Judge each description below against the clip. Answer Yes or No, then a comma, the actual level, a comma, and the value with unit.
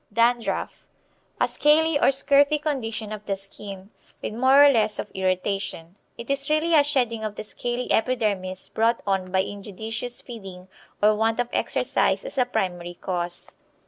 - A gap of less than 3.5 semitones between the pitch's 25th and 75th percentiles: No, average, 5.0 semitones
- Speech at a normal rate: Yes, average, 160 wpm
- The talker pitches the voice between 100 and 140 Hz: No, high, 225 Hz